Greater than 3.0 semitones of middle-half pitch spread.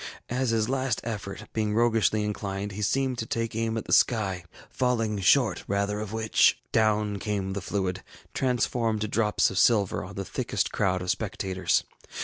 No: narrow, 2.6 semitones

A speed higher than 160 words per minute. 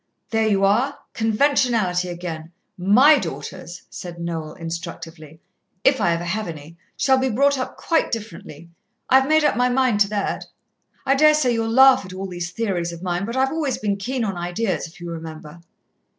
Yes: average, 180 wpm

